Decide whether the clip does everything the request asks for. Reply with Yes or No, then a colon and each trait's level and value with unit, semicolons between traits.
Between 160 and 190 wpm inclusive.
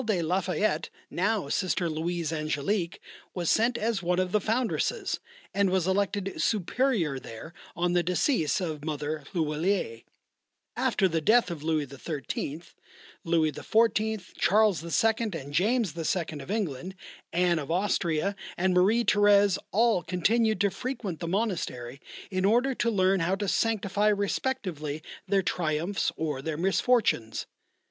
No: average, 140 wpm